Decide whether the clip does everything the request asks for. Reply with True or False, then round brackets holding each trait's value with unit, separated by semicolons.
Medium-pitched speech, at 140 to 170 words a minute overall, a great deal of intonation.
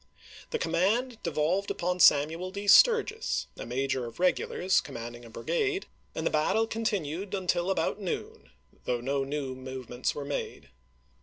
True (170 Hz; 150 wpm; 6.9 semitones)